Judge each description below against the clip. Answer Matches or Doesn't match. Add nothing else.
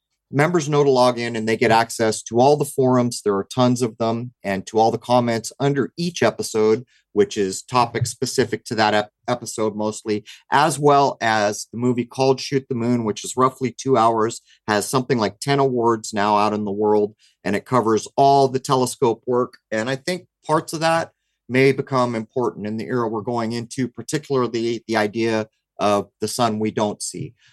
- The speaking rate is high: Doesn't match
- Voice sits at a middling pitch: Doesn't match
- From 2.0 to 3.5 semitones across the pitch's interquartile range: Matches